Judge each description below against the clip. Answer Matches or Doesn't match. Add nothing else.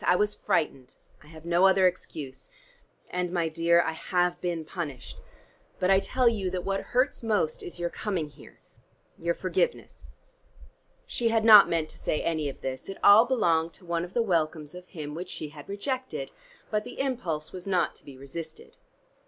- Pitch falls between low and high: Matches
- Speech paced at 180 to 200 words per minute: Matches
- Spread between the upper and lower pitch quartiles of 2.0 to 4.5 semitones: Matches